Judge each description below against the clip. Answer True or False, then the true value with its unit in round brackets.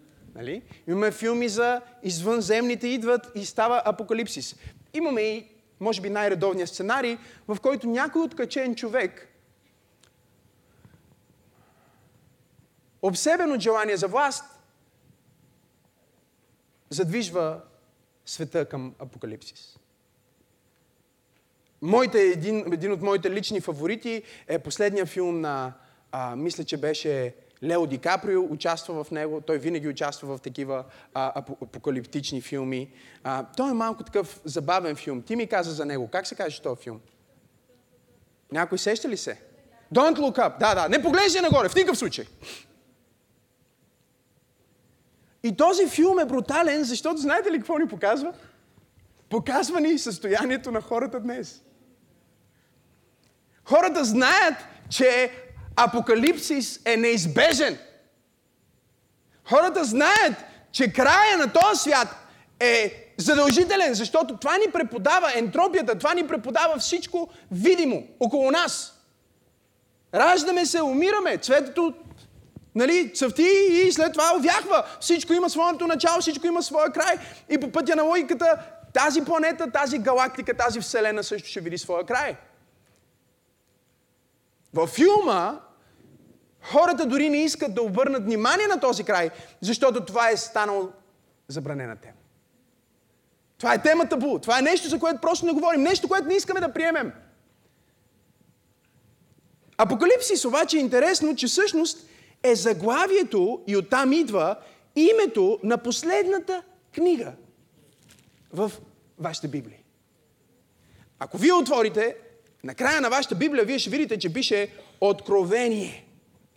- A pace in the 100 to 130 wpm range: True (120 wpm)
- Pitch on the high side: True (240 Hz)